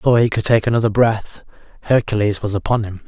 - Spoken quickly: No, average, 195 wpm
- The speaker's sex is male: Yes, male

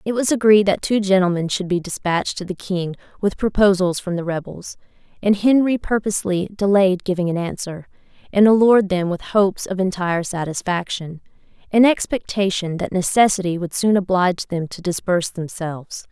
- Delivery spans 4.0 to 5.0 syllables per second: No, 5.5 syllables/s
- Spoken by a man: No, female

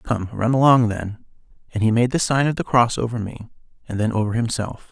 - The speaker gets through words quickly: Yes, fast, 220 wpm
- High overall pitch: No, low, 115 Hz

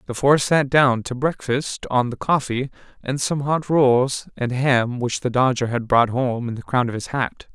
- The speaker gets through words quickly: Yes, fast, 215 wpm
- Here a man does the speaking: Yes, male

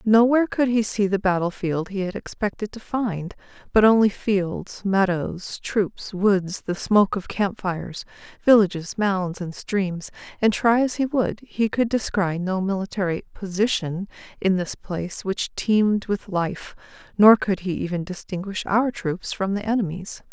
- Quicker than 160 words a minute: No, average, 155 wpm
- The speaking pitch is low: No, high, 200 Hz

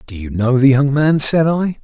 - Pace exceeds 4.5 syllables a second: Yes, 4.7 syllables/s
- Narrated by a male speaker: Yes, male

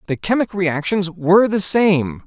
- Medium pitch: Yes, medium, 180 Hz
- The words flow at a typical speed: Yes, average, 160 wpm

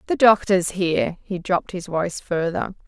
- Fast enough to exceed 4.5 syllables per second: Yes, 5.3 syllables/s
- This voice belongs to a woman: Yes, female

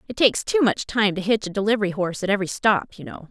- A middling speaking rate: No, fast, 270 wpm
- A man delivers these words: No, female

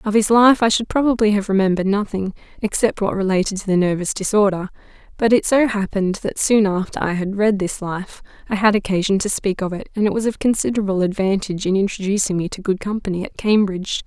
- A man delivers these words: No, female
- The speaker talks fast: Yes, fast, 210 wpm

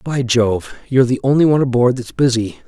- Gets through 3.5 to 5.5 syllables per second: No, 5.9 syllables/s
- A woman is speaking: No, male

